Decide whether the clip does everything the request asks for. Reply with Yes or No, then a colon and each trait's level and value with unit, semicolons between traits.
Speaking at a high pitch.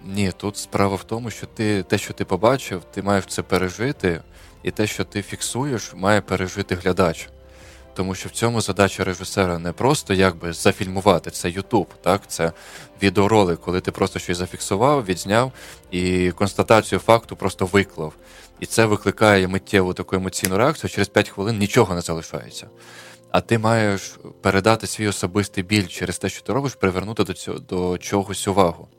No: very low, 95 Hz